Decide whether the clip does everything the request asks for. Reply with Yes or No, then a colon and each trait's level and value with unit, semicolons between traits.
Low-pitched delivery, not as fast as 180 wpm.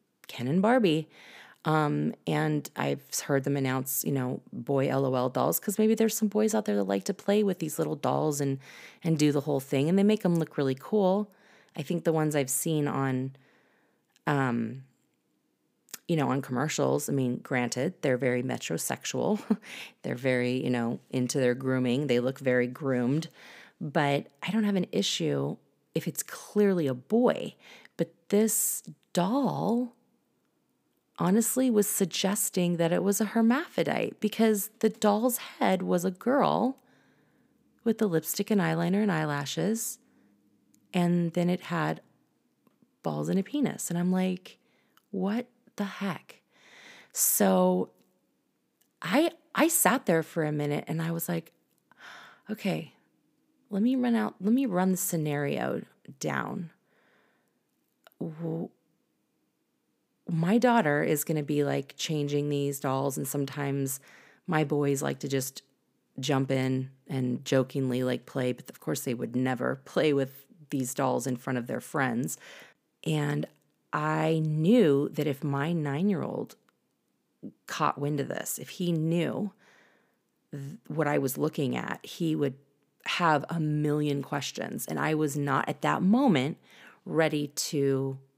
No: medium, 155 Hz; average, 150 wpm